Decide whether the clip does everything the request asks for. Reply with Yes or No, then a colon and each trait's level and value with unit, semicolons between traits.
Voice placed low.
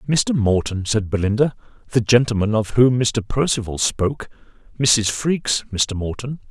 Yes: low, 115 Hz